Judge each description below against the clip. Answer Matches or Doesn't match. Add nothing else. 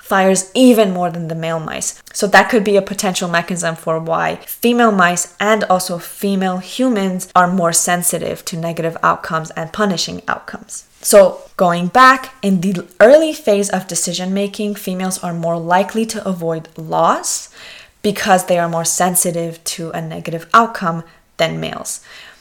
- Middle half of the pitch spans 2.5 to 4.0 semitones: Matches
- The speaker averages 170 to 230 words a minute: Doesn't match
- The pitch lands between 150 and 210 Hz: Matches